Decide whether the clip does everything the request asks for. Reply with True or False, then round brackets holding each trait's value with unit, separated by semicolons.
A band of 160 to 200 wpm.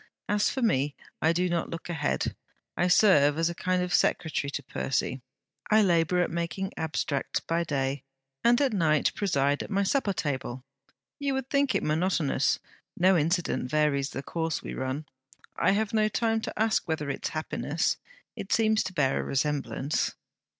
True (170 wpm)